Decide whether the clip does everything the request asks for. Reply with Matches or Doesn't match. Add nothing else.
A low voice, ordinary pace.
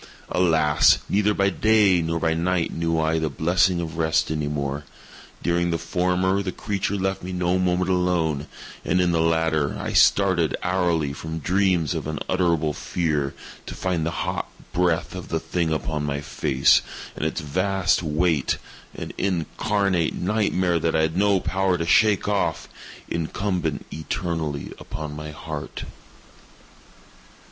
Matches